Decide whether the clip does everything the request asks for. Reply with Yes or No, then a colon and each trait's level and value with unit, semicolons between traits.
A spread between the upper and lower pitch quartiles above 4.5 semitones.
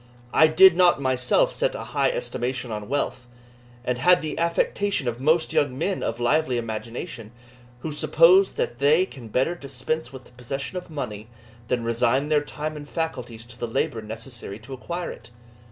Yes: average, 5.0 semitones